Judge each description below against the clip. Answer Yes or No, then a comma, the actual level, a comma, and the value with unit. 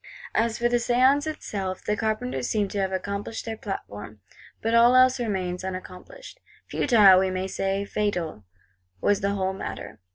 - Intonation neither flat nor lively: Yes, average, 3.8 semitones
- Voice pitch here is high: Yes, high, 200 Hz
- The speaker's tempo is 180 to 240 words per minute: No, average, 160 wpm